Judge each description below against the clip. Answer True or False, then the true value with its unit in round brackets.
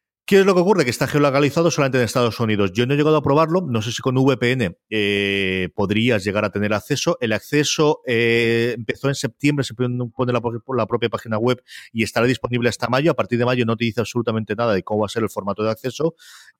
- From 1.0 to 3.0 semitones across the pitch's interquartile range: False (3.7 semitones)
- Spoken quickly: True (235 wpm)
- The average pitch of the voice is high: False (120 Hz)